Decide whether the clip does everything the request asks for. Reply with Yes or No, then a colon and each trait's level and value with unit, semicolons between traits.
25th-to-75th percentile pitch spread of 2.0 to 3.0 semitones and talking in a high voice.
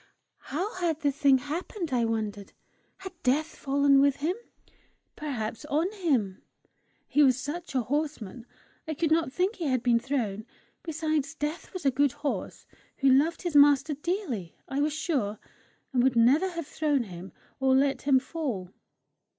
No: average, 3.9 semitones; very high, 285 Hz